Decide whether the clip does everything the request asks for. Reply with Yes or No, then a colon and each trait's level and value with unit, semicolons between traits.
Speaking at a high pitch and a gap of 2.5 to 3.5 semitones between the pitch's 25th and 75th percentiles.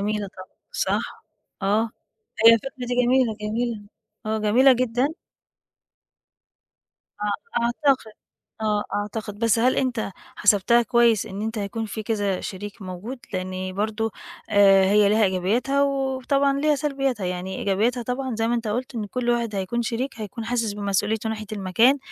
Yes: high, 220 Hz; average, 3.2 semitones